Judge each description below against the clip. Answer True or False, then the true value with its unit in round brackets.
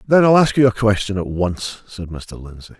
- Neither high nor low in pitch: False (105 Hz)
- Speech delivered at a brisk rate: True (235 wpm)